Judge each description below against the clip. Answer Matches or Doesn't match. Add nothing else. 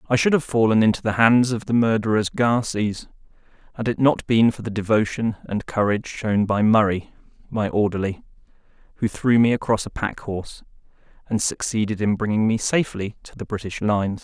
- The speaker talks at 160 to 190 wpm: Matches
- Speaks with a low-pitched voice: Matches